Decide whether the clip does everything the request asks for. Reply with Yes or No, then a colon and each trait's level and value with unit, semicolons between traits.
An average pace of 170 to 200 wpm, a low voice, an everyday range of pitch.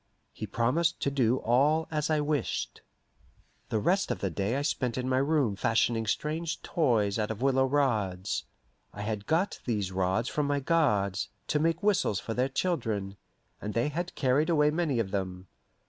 No: average, 180 wpm; low, 130 Hz; wide, 6.2 semitones